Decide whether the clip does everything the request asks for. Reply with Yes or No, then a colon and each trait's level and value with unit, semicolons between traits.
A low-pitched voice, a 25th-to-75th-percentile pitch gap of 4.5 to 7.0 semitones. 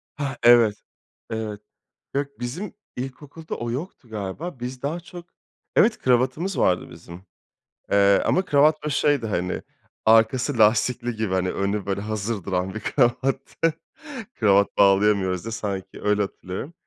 Yes: low, 115 Hz; wide, 5.4 semitones